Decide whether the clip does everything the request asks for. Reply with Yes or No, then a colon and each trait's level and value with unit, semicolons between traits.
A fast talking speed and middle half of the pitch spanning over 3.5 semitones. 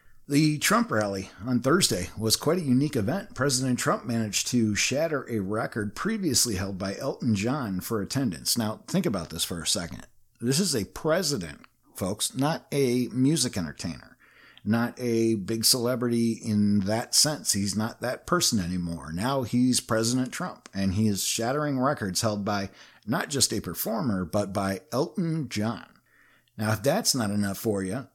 No: average, 165 wpm; average, 4.3 semitones